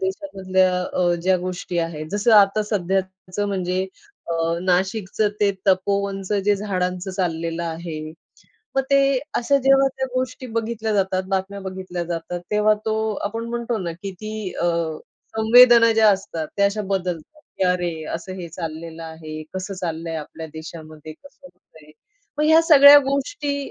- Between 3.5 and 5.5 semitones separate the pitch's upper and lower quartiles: Yes, average, 4.0 semitones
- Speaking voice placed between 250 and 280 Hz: No, high, 190 Hz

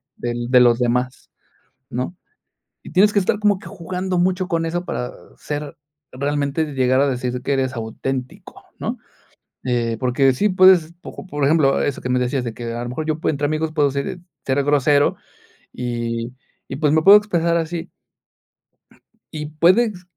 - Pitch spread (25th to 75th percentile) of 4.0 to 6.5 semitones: Yes, average, 5.1 semitones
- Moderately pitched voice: Yes, medium, 145 Hz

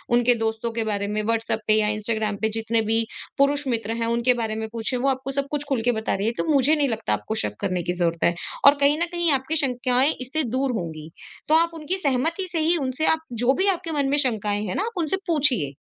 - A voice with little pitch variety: No, average, 5.0 semitones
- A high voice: Yes, very high, 250 Hz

